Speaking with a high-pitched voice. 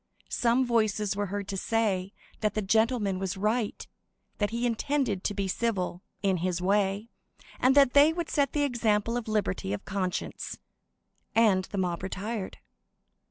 Yes: high, 210 Hz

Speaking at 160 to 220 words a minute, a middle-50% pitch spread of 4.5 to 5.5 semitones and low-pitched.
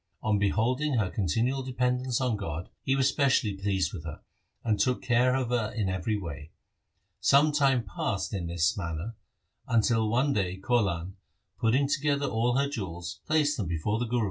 Yes: average, 170 wpm; average, 5.2 semitones; low, 115 Hz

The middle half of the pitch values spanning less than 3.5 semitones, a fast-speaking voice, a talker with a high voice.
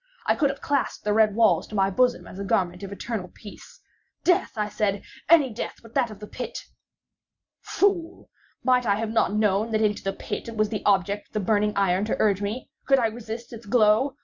Yes: average, 3.1 semitones; fast, 220 wpm; high, 215 Hz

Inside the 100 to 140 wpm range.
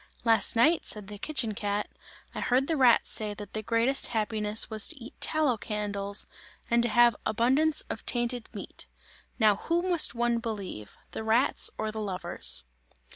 No: average, 170 wpm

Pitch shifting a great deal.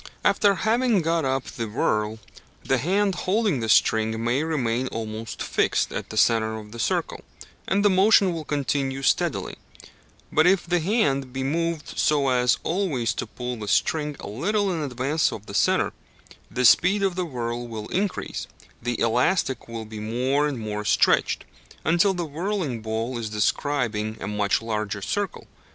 Yes: wide, 7.4 semitones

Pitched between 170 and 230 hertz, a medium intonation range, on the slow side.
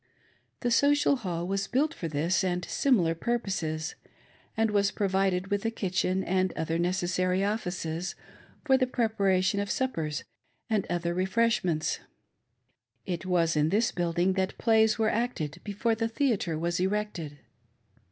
No: high, 190 Hz; average, 4.3 semitones; average, 145 wpm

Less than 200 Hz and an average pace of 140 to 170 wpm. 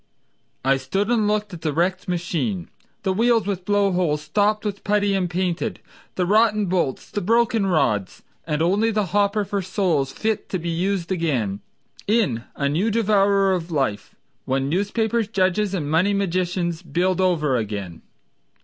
Yes: medium, 185 Hz; average, 160 wpm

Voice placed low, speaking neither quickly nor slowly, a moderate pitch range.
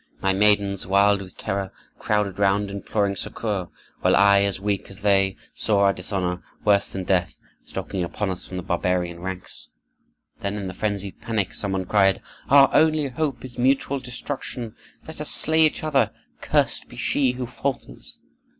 Yes: low, 100 Hz; average, 170 wpm; average, 4.1 semitones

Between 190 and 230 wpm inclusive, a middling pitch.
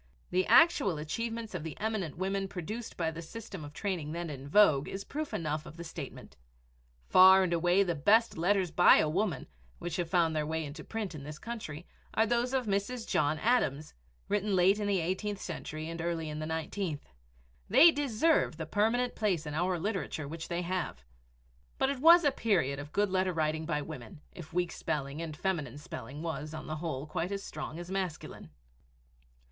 Yes: average, 195 wpm; medium, 175 Hz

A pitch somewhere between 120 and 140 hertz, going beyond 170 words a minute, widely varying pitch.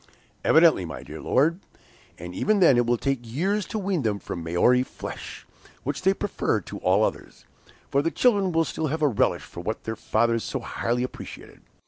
Yes: low, 135 Hz; average, 190 wpm; wide, 7.9 semitones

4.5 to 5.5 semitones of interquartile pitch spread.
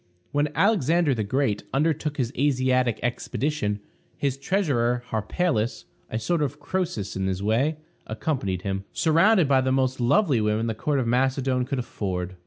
Yes: average, 5.1 semitones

